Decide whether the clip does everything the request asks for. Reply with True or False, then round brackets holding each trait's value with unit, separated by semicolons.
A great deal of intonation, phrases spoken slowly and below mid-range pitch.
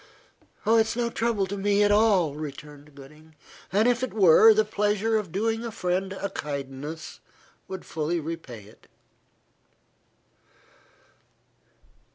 False (6.0 semitones; 130 wpm; 190 Hz)